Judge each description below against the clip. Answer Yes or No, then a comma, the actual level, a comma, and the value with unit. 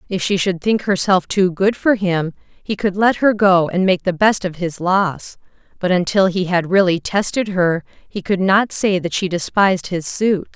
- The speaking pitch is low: No, high, 190 Hz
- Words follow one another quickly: Yes, fast, 210 wpm